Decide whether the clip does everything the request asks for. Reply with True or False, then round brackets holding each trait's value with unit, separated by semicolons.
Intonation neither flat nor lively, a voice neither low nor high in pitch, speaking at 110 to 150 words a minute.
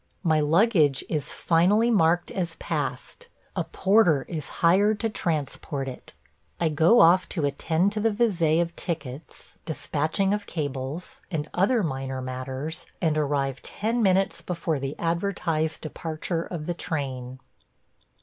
True (4.5 semitones; 165 Hz; 140 wpm)